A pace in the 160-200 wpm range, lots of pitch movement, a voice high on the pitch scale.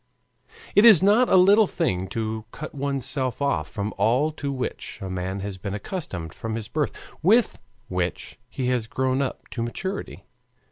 No: average, 175 wpm; wide, 7.5 semitones; low, 130 Hz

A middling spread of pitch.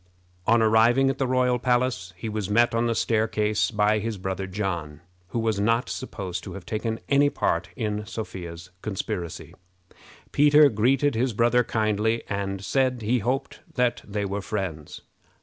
Yes: average, 3.7 semitones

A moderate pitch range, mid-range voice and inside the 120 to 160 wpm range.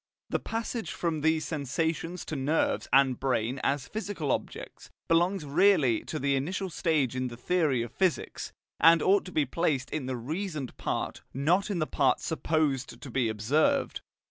No: average, 4.7 semitones; medium, 155 Hz; average, 170 wpm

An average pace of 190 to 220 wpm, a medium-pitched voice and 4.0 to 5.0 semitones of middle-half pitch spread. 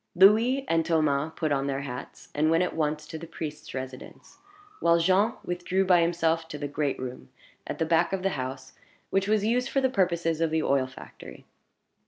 Yes: average, 200 wpm; medium, 165 Hz; average, 4.3 semitones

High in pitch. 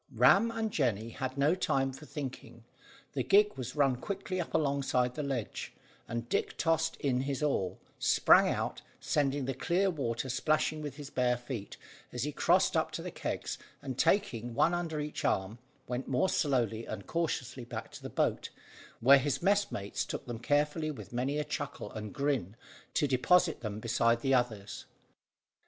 No: low, 135 Hz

